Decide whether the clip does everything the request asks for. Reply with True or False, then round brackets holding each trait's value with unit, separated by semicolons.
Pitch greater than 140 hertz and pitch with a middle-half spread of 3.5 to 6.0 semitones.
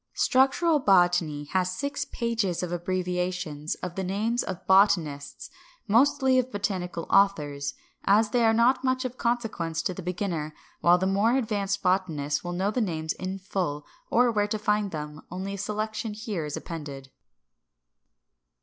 True (190 Hz; 4.1 semitones)